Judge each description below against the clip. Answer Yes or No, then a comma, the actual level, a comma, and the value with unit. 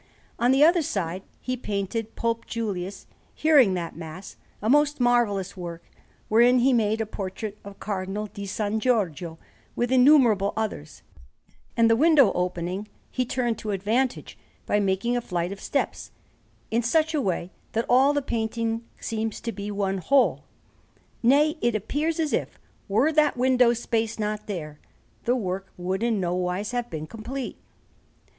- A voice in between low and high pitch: No, high, 220 Hz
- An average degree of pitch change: Yes, average, 4.3 semitones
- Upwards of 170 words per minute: No, average, 155 wpm